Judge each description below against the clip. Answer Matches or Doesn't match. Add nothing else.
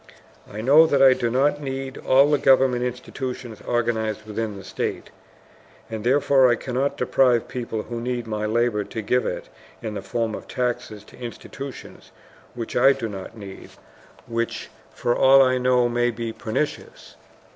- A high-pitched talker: Doesn't match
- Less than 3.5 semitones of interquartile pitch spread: Matches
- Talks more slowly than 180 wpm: Matches